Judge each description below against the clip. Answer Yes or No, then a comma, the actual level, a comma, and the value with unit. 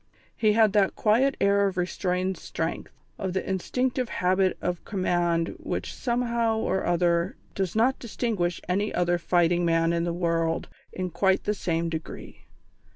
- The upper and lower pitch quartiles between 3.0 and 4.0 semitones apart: Yes, average, 3.4 semitones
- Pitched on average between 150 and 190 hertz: Yes, medium, 185 Hz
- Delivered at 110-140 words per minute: No, average, 155 wpm